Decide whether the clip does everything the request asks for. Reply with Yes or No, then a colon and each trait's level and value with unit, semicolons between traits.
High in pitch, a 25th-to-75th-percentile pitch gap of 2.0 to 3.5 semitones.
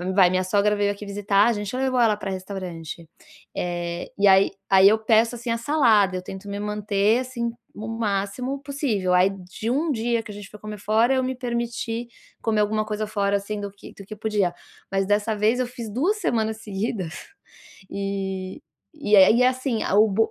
Yes: high, 210 Hz; average, 2.9 semitones